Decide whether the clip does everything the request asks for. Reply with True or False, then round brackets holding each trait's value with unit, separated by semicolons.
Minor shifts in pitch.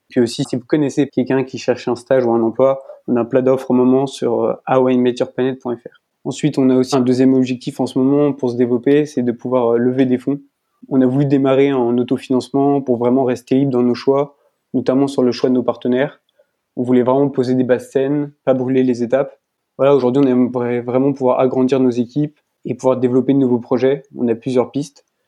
True (1.5 semitones)